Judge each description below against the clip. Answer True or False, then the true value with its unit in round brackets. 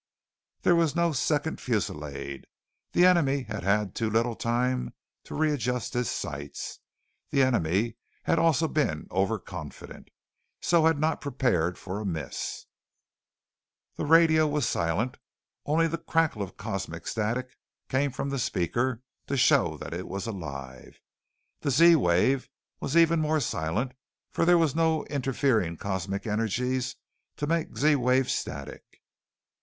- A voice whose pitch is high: False (125 Hz)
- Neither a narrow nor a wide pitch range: False (7.7 semitones)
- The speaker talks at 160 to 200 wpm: False (140 wpm)